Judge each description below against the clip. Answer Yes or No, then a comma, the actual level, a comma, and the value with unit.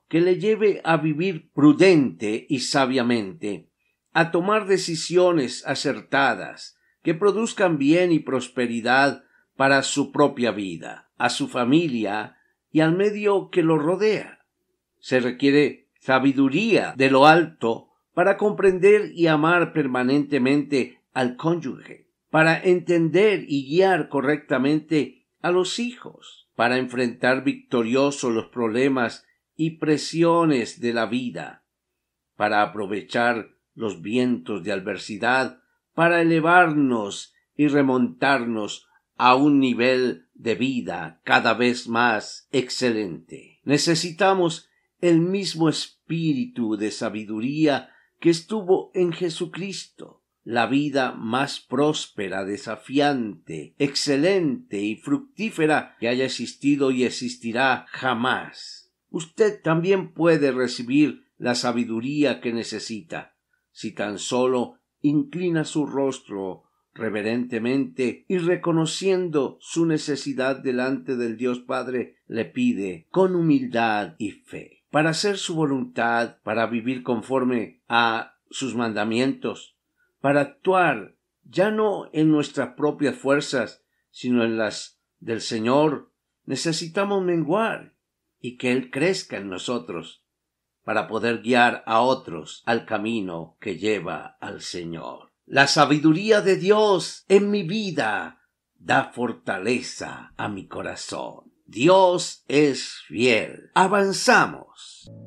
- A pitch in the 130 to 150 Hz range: Yes, medium, 140 Hz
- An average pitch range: No, wide, 5.8 semitones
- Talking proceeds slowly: Yes, slow, 110 wpm